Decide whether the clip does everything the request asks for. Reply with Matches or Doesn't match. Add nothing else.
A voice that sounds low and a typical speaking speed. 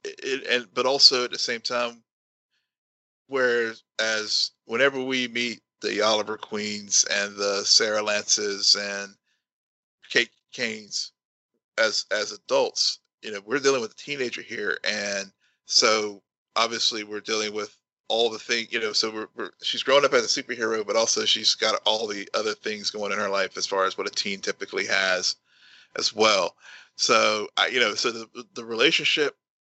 Matches